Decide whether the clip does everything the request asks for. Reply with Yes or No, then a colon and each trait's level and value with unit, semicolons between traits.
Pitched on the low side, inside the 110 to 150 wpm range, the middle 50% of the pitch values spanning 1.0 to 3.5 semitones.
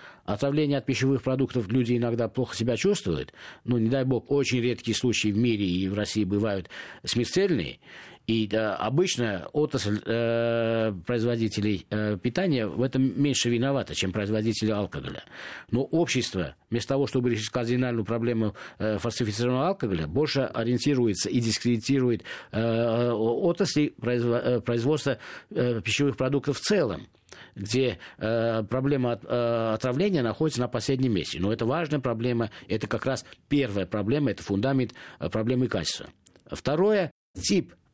Yes: low, 120 Hz; average, 140 wpm; average, 3.2 semitones